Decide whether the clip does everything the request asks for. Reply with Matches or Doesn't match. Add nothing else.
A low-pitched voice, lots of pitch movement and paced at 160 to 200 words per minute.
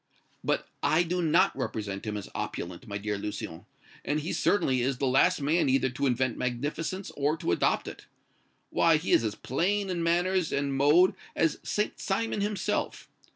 Doesn't match